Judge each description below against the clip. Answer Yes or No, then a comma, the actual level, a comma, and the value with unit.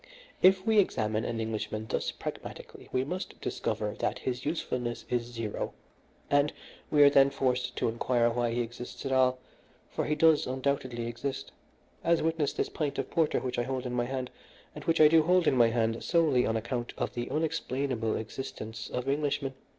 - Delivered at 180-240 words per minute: Yes, average, 185 wpm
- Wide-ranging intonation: No, average, 3.7 semitones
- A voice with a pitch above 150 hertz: No, low, 130 Hz